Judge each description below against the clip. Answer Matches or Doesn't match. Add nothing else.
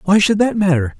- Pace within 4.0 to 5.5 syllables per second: Doesn't match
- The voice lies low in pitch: Doesn't match